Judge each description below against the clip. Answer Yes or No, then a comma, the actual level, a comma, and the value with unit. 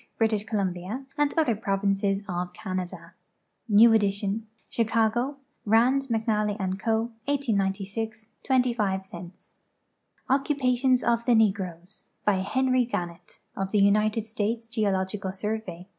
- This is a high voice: Yes, high, 215 Hz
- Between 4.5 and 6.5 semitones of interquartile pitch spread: No, average, 3.3 semitones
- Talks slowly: Yes, slow, 115 wpm